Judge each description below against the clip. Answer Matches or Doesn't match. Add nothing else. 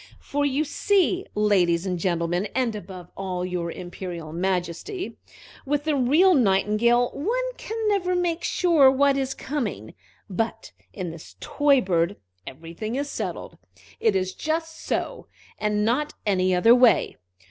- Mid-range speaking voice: Doesn't match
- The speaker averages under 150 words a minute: Matches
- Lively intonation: Matches